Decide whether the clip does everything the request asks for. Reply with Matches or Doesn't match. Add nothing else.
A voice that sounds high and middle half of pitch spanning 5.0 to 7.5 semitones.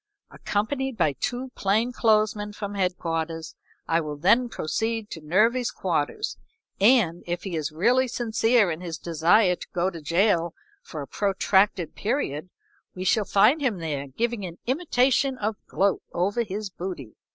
Matches